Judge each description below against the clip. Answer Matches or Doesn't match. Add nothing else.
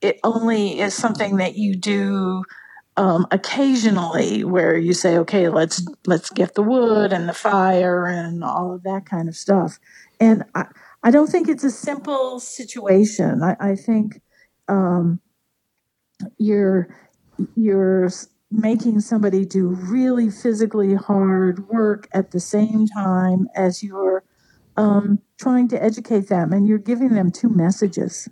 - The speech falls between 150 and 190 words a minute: Doesn't match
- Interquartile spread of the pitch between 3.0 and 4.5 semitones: Matches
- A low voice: Doesn't match